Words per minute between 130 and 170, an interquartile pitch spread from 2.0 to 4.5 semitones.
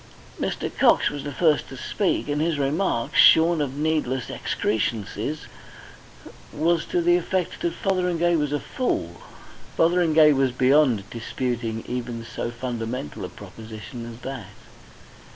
No: slow, 135 wpm; wide, 5.6 semitones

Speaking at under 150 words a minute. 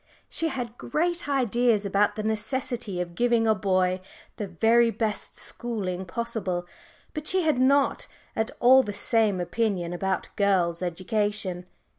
Yes: average, 140 wpm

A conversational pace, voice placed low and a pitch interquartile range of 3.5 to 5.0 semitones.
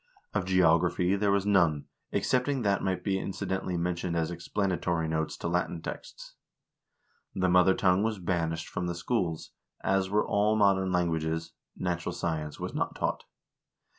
No: average, 150 wpm; very low, 90 Hz; narrow, 2.5 semitones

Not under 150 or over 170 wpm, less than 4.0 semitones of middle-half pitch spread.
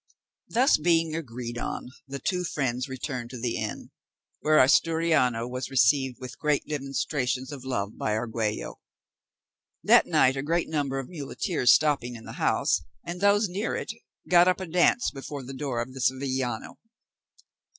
No: average, 160 wpm; average, 4.5 semitones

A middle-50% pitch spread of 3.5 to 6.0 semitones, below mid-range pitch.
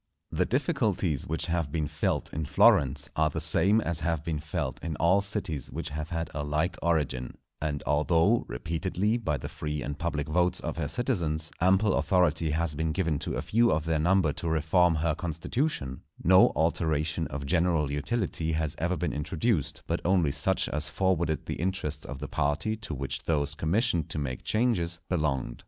No: average, 3.1 semitones; very low, 80 Hz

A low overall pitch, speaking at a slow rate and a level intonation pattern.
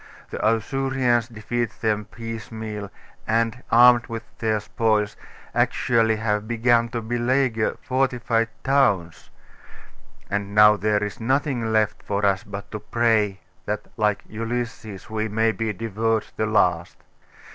Yes: low, 110 Hz; slow, 125 wpm; narrow, 1.9 semitones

